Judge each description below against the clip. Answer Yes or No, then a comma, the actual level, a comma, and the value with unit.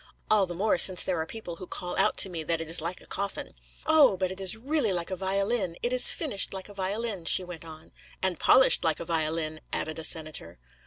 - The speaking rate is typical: No, fast, 235 wpm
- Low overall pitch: No, medium, 185 Hz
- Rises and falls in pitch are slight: No, average, 3.5 semitones